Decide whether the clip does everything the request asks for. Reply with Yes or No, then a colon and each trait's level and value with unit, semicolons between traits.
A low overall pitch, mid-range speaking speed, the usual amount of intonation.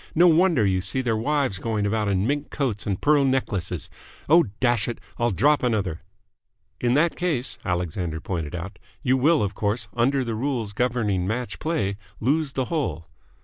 No: low, 120 Hz; average, 175 wpm; wide, 5.8 semitones